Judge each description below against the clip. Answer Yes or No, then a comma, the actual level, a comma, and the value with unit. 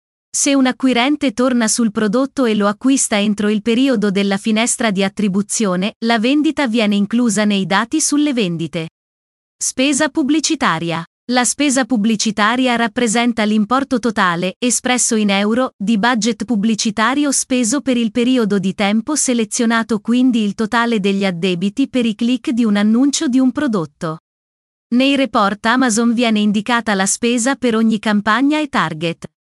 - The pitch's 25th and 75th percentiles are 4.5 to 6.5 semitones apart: No, average, 3.6 semitones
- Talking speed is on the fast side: No, average, 145 wpm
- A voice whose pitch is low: No, high, 230 Hz